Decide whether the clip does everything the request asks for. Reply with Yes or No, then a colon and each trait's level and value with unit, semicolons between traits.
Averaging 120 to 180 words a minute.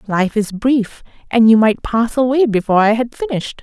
No: average, 200 wpm